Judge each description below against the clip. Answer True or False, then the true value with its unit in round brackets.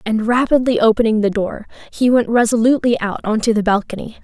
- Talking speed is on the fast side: False (170 wpm)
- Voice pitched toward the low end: False (225 Hz)